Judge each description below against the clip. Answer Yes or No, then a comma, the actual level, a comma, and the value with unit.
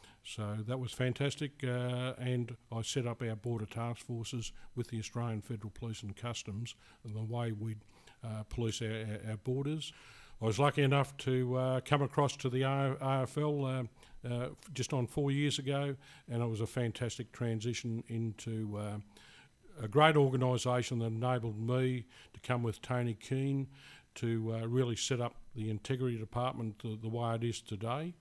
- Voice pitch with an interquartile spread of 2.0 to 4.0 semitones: Yes, narrow, 2.6 semitones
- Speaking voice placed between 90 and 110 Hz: No, low, 120 Hz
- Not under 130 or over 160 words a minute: No, average, 170 wpm